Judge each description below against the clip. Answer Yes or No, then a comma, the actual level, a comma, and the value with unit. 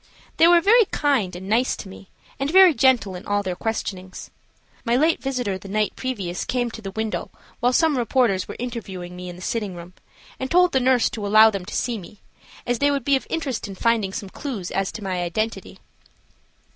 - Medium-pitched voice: No, high, 225 Hz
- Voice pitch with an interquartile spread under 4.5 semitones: No, average, 5.3 semitones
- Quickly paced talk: Yes, fast, 210 wpm